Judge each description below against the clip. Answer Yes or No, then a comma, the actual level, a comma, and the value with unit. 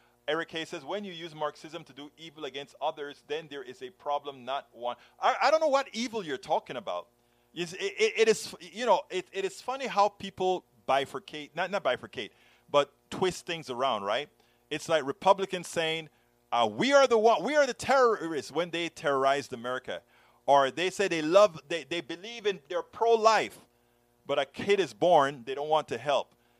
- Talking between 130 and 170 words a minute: No, average, 195 wpm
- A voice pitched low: No, medium, 170 Hz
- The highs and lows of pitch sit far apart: Yes, wide, 6.9 semitones